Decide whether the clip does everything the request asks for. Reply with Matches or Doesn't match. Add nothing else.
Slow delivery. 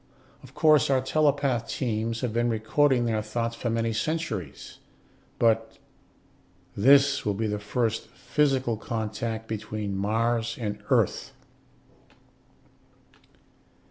Matches